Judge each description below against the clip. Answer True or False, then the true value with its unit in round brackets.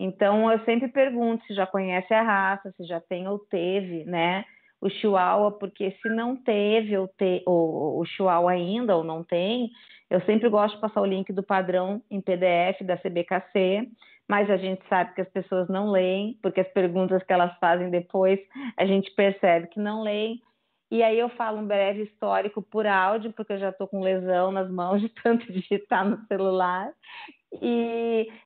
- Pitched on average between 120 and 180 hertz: False (195 Hz)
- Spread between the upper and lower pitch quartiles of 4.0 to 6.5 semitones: False (2.7 semitones)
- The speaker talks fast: True (190 wpm)